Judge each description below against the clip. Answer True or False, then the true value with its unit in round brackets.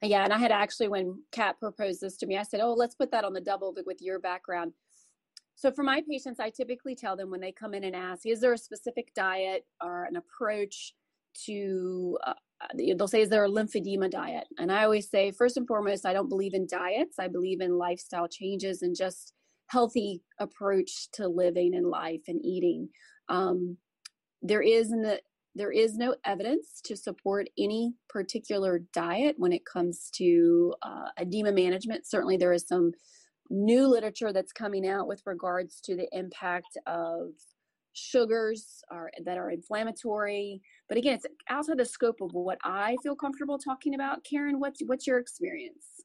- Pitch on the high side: True (205 Hz)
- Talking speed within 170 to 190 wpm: True (180 wpm)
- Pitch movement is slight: False (4.8 semitones)